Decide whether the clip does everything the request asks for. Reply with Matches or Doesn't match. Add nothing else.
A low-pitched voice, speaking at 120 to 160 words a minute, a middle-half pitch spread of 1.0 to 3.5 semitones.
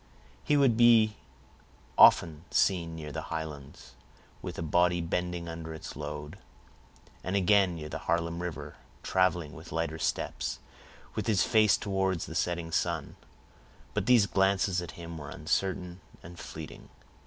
Matches